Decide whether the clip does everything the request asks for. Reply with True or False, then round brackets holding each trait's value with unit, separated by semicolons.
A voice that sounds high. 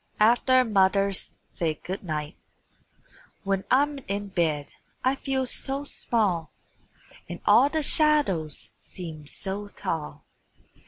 True (200 Hz)